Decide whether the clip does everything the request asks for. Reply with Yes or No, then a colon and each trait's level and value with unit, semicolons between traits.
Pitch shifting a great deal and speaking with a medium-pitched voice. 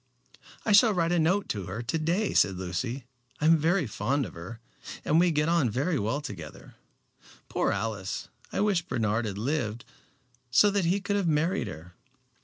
Yes: wide, 8.2 semitones; medium, 145 Hz